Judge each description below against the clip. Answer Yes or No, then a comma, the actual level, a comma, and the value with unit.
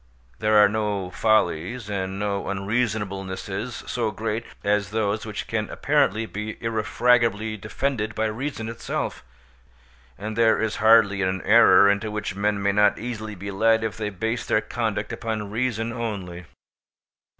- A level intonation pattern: Yes, narrow, 1.9 semitones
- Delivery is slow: No, average, 145 wpm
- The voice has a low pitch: Yes, low, 105 Hz